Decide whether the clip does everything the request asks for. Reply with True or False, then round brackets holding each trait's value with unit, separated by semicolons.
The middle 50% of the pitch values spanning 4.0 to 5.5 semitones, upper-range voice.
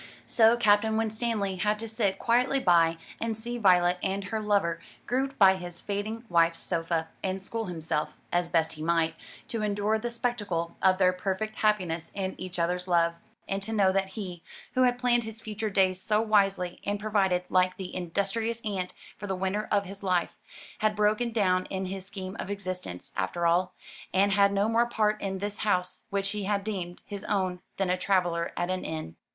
False (2.9 semitones; 195 Hz)